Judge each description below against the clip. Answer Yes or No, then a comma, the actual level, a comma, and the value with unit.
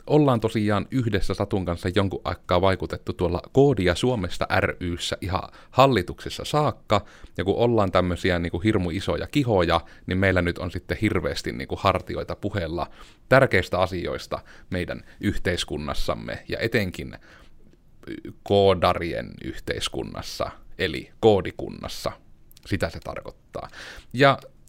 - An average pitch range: Yes, average, 3.4 semitones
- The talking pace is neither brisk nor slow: Yes, average, 115 wpm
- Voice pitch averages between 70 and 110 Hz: Yes, very low, 95 Hz